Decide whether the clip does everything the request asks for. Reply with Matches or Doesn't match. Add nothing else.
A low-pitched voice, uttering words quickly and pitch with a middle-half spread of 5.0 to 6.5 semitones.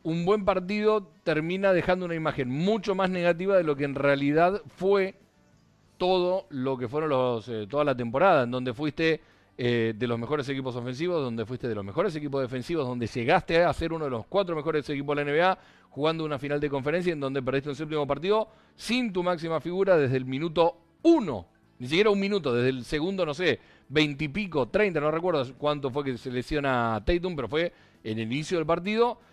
Doesn't match